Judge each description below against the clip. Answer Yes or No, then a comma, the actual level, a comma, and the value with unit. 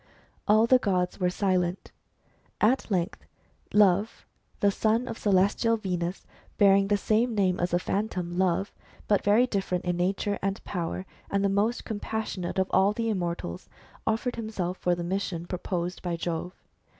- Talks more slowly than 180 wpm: Yes, average, 155 wpm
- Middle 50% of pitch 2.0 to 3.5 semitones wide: Yes, average, 2.9 semitones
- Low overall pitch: No, high, 195 Hz